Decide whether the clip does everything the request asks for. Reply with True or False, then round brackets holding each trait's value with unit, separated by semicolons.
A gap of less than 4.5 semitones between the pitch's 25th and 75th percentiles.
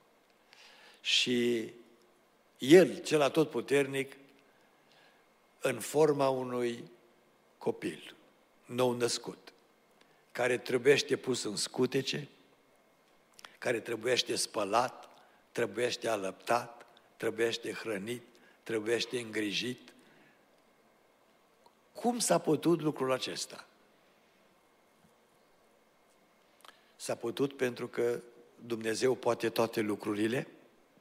True (2.7 semitones)